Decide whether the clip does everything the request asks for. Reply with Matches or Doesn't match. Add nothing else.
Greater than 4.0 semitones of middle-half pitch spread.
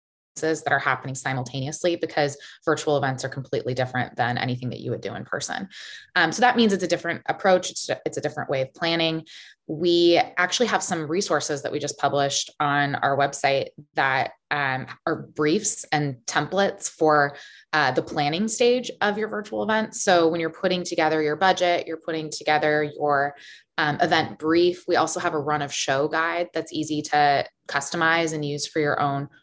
Doesn't match